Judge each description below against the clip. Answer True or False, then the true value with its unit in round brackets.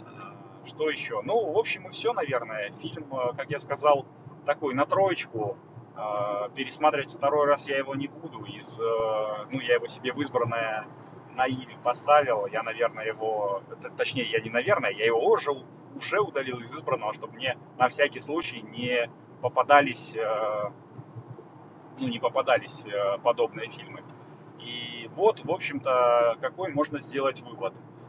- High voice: False (135 Hz)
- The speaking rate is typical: True (140 wpm)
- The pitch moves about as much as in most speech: True (4.4 semitones)